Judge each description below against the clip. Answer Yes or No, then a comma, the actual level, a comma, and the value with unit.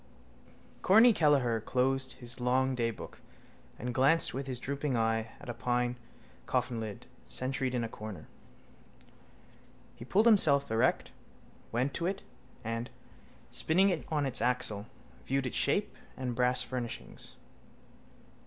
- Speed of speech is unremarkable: No, slow, 130 wpm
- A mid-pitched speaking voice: No, low, 125 Hz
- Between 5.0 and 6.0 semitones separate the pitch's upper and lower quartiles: No, narrow, 2.6 semitones